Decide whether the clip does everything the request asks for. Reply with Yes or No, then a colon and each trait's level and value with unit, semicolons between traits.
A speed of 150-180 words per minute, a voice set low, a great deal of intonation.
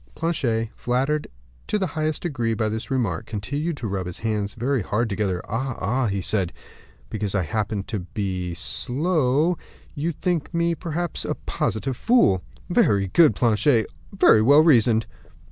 Yes: average, 160 wpm; low, 115 Hz; wide, 6.7 semitones